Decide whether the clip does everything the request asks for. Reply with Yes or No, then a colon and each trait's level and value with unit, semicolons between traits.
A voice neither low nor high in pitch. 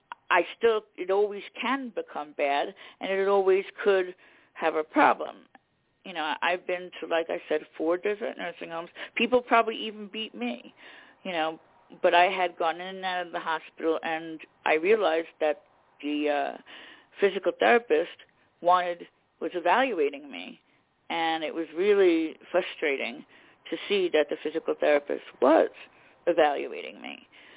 Yes: medium, 180 Hz